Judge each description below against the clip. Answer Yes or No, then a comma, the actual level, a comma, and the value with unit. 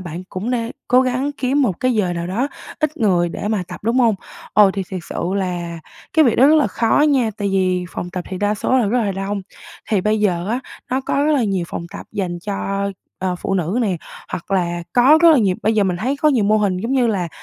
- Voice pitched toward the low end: No, high, 205 Hz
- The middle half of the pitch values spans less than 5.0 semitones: No, average, 5.3 semitones